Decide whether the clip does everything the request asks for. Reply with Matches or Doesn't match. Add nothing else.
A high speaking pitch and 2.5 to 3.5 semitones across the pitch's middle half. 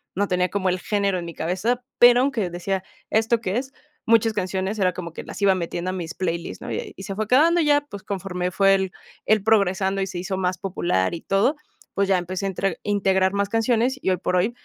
Matches